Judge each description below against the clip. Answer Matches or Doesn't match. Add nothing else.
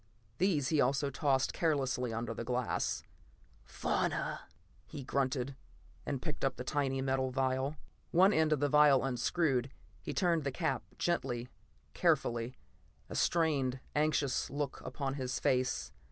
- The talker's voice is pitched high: Doesn't match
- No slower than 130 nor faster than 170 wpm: Matches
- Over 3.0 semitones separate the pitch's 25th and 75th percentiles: Doesn't match